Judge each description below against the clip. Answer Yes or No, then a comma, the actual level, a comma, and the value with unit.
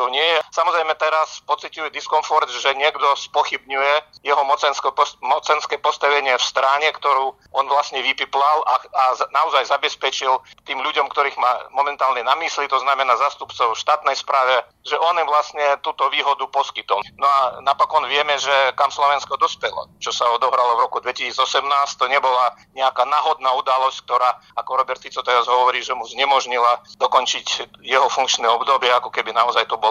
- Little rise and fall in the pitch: Yes, narrow, 2.1 semitones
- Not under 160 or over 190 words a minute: Yes, fast, 165 wpm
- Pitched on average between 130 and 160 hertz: Yes, medium, 140 Hz